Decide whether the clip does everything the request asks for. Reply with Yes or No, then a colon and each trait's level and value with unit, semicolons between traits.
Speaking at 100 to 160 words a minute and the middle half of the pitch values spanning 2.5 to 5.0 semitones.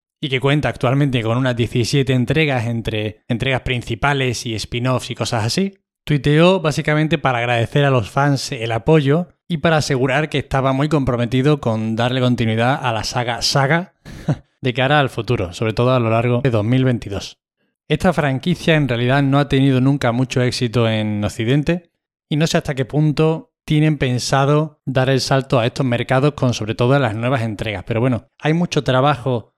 No: average, 175 wpm; average, 3.7 semitones